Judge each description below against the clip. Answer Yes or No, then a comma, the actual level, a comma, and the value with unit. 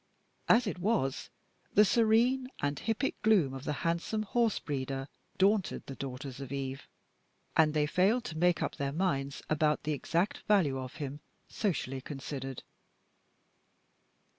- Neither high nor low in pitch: Yes, medium, 155 Hz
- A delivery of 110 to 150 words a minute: Yes, average, 140 wpm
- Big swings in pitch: Yes, wide, 7.1 semitones